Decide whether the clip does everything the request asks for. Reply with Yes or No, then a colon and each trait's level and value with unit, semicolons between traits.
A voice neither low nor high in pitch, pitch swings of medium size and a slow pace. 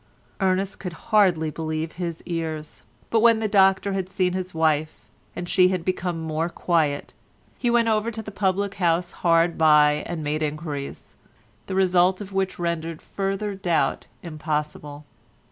No: medium, 175 Hz; average, 3.4 semitones; average, 155 wpm